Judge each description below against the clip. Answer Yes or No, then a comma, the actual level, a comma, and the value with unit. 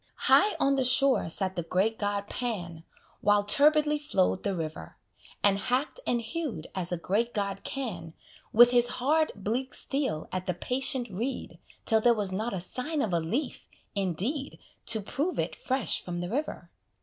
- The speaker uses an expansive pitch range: Yes, wide, 6.0 semitones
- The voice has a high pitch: Yes, high, 220 Hz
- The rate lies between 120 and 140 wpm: No, average, 175 wpm